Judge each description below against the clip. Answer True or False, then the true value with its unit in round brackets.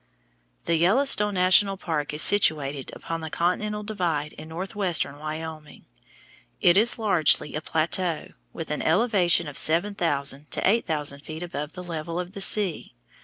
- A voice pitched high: False (170 Hz)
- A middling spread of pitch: True (4.1 semitones)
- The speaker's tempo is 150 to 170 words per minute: True (155 wpm)